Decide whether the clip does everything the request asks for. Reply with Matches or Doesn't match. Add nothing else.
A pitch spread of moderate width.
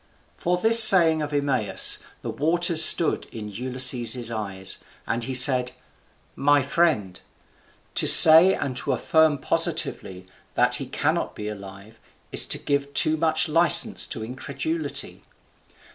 Doesn't match